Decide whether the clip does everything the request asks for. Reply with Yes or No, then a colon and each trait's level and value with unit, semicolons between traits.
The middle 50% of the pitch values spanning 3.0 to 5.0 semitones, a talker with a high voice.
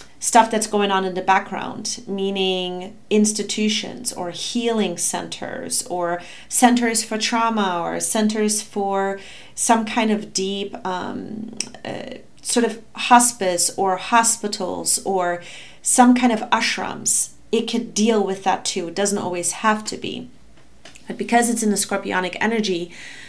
Yes: average, 3.3 semitones; high, 210 Hz